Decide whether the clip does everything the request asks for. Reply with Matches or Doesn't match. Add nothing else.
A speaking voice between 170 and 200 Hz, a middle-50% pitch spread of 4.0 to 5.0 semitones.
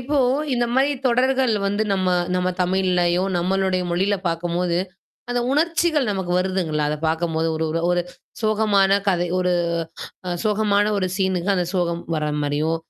Doesn't match